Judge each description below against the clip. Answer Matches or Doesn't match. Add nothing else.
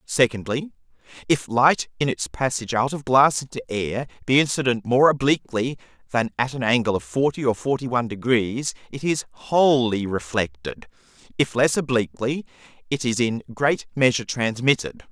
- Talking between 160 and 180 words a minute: Doesn't match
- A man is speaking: Matches